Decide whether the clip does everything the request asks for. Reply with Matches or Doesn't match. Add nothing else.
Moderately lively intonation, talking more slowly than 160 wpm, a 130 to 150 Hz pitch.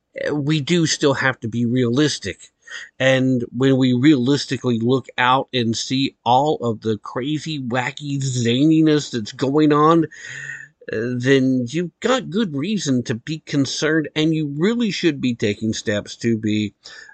Matches